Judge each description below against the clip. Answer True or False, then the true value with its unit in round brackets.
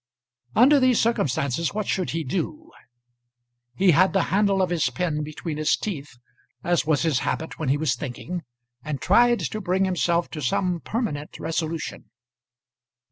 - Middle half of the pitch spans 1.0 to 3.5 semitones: False (4.3 semitones)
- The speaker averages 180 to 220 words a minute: False (155 wpm)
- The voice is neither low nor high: True (170 Hz)